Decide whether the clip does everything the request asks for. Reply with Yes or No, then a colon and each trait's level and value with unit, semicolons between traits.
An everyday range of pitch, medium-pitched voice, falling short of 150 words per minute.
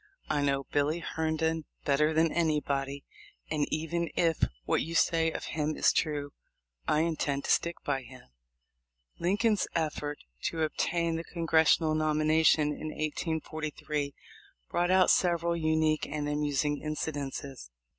No: narrow, 1.9 semitones; medium, 155 Hz; slow, 135 wpm